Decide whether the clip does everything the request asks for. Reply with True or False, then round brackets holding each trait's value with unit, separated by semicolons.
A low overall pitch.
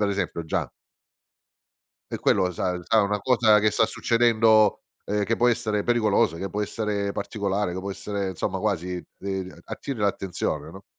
True (100 Hz)